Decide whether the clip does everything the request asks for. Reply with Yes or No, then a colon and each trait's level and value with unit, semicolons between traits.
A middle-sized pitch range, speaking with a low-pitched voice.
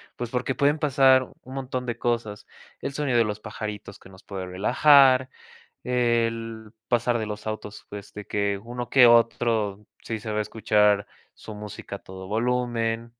Yes: average, 3.0 semitones; low, 115 Hz